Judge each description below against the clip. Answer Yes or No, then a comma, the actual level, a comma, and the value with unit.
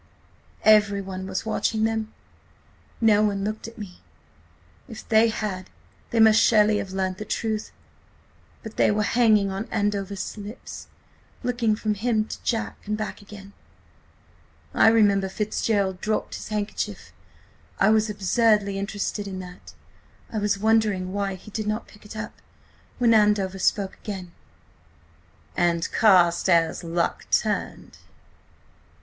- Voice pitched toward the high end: Yes, high, 210 Hz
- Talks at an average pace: No, slow, 130 wpm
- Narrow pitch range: Yes, narrow, 2.2 semitones